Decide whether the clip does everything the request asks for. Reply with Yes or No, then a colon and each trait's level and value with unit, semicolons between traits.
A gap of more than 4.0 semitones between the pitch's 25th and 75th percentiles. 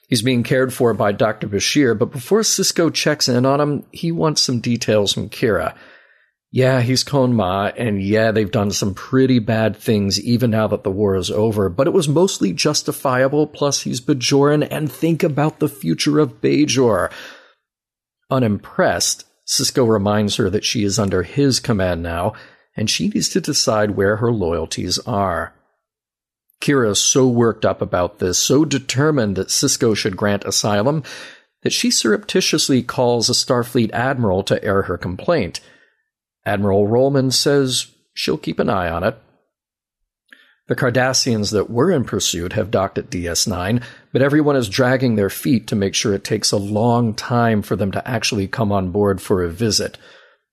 Yes: average, 4.9 semitones